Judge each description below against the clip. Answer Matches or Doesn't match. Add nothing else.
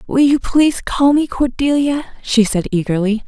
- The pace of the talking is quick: Doesn't match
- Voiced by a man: Doesn't match